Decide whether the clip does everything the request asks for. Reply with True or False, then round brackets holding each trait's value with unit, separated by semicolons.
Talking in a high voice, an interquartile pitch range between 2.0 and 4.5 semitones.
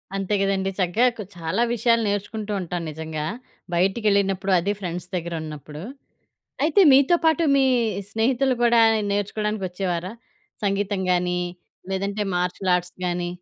True (195 Hz; 3.3 semitones)